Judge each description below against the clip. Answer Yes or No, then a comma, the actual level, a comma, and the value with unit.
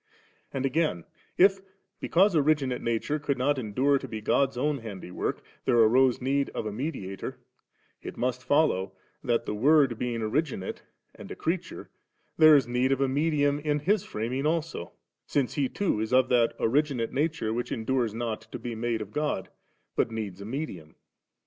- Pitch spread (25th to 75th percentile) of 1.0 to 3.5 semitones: No, average, 4.6 semitones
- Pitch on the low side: Yes, low, 130 Hz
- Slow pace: No, average, 170 wpm